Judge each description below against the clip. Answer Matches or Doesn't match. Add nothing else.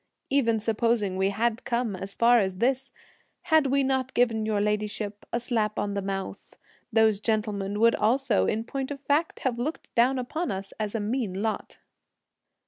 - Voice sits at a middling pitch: Doesn't match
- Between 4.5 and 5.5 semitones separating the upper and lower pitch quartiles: Doesn't match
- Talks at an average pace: Matches